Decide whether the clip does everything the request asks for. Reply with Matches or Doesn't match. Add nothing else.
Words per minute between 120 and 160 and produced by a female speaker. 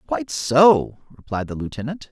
Doesn't match